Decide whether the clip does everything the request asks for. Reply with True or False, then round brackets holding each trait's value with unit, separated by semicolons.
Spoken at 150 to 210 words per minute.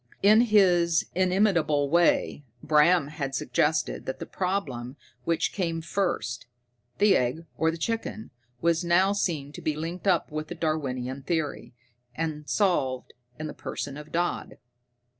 False (140 wpm)